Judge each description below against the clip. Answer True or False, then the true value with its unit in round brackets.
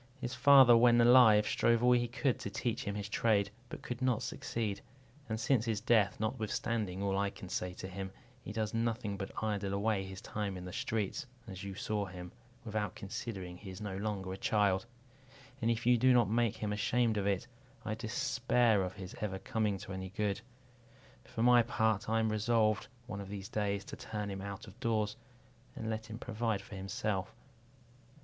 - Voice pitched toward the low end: True (105 Hz)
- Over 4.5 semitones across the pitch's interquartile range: False (2.7 semitones)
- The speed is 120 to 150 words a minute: False (195 wpm)